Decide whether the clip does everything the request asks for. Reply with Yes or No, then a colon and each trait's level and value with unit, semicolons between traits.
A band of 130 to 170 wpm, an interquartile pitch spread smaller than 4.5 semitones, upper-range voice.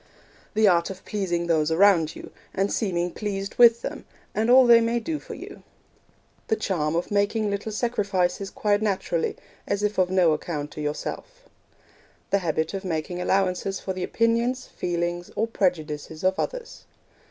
Yes: average, 165 wpm; average, 3.9 semitones; high, 195 Hz